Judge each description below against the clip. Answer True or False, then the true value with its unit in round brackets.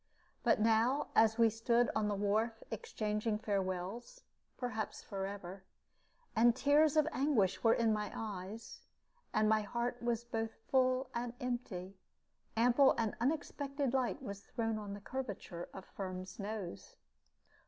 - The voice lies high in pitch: True (225 Hz)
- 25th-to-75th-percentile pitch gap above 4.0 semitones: False (3.2 semitones)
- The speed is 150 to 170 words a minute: False (135 wpm)